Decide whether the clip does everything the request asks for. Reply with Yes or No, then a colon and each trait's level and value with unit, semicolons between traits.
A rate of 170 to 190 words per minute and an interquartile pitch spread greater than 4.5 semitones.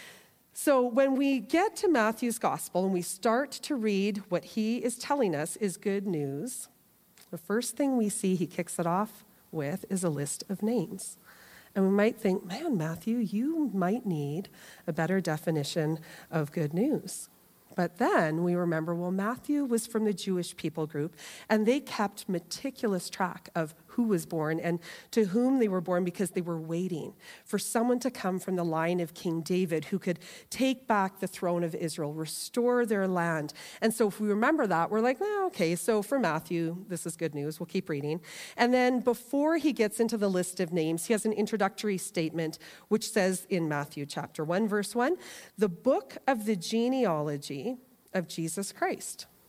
Yes: average, 185 wpm; average, 5.3 semitones